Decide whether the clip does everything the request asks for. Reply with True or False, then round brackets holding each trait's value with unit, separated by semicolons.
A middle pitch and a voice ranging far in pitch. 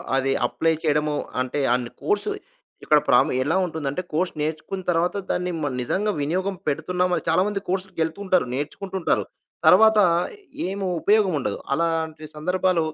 False (165 Hz; 3.8 semitones)